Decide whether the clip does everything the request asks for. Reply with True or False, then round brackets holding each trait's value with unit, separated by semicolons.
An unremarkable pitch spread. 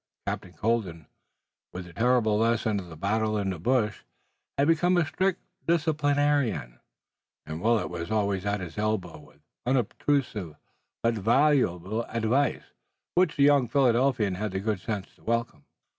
False (6.1 semitones)